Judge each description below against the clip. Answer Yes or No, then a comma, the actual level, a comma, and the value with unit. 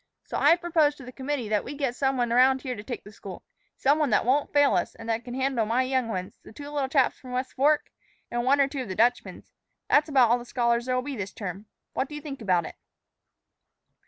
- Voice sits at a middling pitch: No, very high, 255 Hz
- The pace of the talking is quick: Yes, fast, 255 wpm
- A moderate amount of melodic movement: Yes, average, 3.4 semitones